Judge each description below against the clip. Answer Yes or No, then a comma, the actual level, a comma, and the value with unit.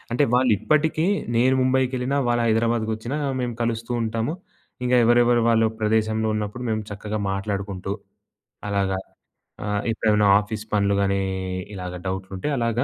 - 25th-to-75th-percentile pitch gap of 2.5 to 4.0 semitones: Yes, average, 2.8 semitones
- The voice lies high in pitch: No, low, 110 Hz